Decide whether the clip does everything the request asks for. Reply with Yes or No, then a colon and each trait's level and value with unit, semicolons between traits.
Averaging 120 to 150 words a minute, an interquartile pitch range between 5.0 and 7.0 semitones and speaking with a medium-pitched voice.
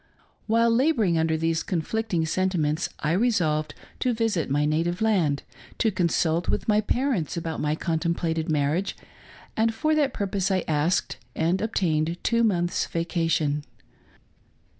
Yes: average, 140 wpm; wide, 5.4 semitones; medium, 175 Hz